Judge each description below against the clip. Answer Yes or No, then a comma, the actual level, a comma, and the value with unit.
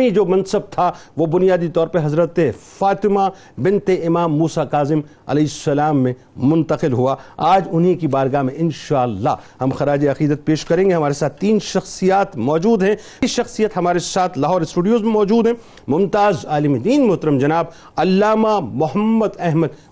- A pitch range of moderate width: Yes, average, 4.7 semitones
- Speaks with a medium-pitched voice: Yes, medium, 170 Hz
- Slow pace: No, average, 160 wpm